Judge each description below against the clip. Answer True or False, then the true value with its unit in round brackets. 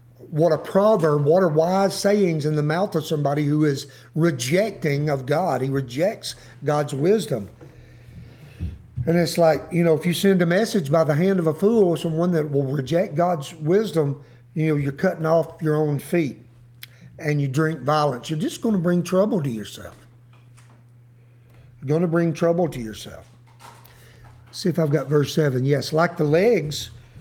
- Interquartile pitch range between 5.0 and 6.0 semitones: True (5.5 semitones)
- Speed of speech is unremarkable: True (180 wpm)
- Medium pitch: True (150 Hz)